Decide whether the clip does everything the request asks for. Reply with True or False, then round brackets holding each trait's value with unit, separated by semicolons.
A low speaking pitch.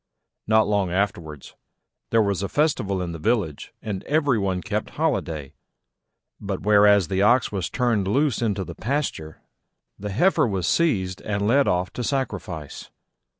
True (100 Hz)